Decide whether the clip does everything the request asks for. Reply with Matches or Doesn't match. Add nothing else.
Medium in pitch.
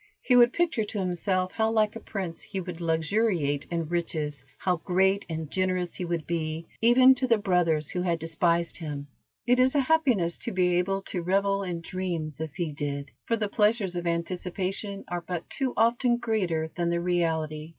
Matches